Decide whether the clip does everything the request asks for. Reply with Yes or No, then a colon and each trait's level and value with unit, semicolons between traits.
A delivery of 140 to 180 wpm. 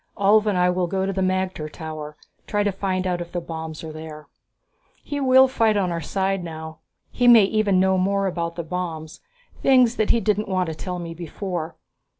No: fast, 205 wpm